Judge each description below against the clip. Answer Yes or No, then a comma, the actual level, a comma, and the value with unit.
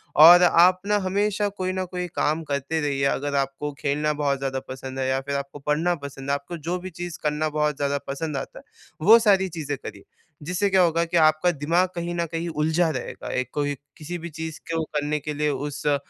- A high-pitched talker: No, medium, 155 Hz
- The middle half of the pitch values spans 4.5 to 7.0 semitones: No, average, 3.5 semitones